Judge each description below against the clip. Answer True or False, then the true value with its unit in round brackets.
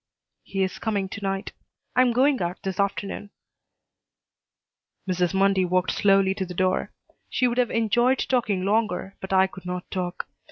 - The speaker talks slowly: False (165 wpm)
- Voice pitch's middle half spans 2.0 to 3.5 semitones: True (2.9 semitones)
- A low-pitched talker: False (195 Hz)